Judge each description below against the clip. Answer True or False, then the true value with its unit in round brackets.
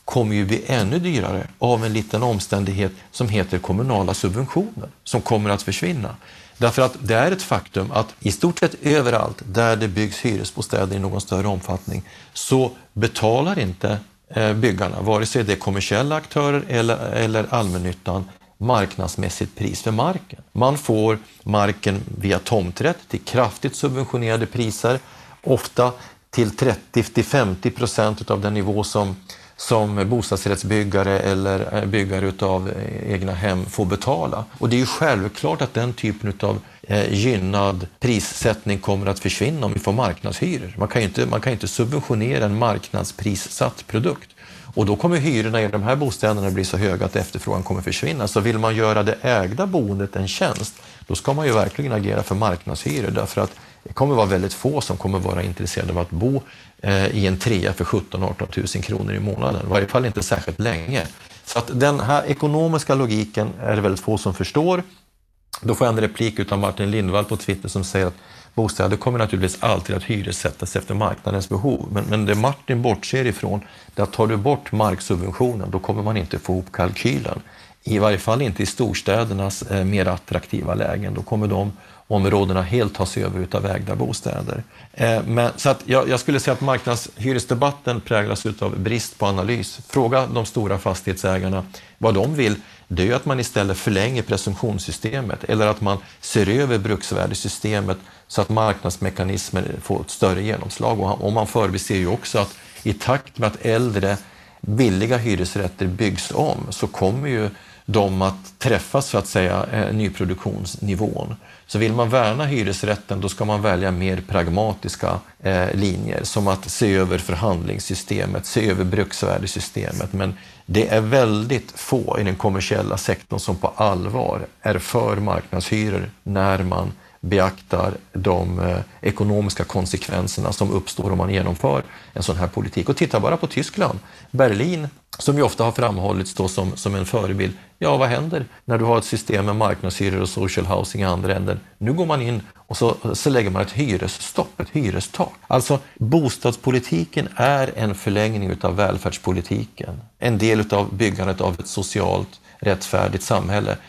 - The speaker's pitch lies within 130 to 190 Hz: False (105 Hz)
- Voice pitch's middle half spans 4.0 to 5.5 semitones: False (3.5 semitones)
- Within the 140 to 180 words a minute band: True (160 wpm)